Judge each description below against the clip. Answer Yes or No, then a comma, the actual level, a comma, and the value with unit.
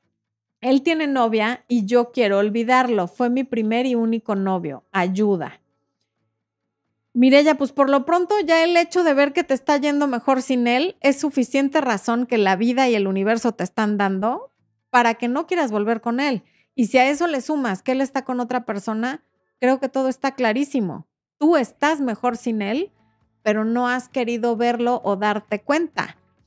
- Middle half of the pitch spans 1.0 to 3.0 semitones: No, average, 4.3 semitones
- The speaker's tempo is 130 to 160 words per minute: No, average, 180 wpm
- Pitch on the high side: Yes, high, 245 Hz